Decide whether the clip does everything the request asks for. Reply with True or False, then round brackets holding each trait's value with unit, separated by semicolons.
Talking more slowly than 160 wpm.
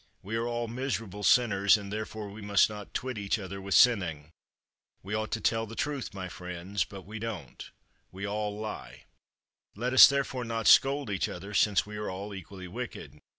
False (190 wpm)